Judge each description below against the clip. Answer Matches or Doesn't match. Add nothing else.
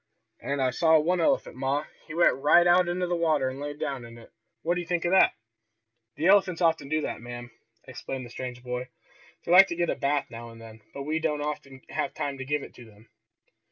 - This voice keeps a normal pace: Doesn't match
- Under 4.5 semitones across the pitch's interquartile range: Doesn't match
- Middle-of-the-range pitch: Matches